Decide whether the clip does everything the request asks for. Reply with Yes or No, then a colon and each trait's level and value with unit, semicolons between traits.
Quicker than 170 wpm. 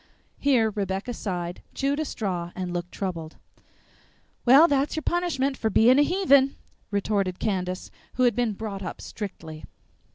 No: average, 150 wpm